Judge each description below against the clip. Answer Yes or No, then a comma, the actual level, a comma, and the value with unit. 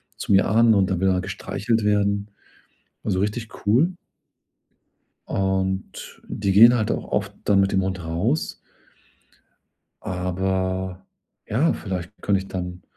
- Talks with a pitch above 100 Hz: No, very low, 95 Hz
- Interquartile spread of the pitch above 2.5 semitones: No, narrow, 1.9 semitones